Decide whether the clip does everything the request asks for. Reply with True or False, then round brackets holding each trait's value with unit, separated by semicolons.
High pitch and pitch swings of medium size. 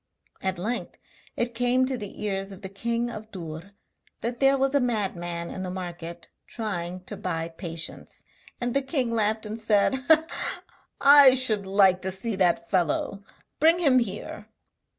True (205 Hz; 4.8 semitones)